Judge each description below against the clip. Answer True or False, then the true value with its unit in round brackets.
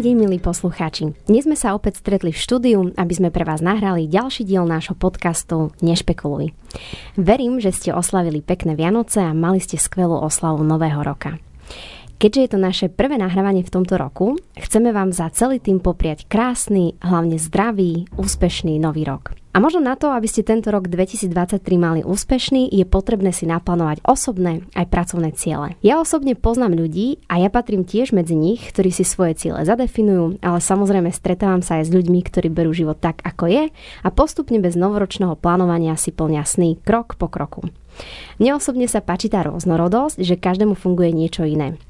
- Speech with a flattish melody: False (4.1 semitones)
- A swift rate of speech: True (175 wpm)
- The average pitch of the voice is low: False (185 Hz)